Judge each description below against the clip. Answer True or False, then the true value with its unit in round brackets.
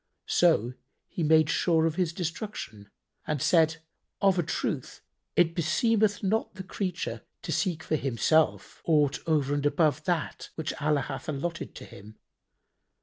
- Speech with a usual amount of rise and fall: True (3.1 semitones)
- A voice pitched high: False (160 Hz)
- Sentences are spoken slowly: False (145 wpm)